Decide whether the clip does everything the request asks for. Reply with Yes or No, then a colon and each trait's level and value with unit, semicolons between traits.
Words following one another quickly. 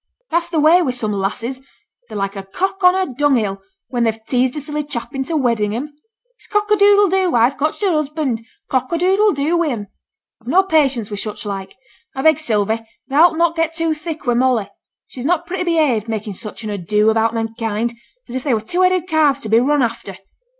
Yes: fast, 220 wpm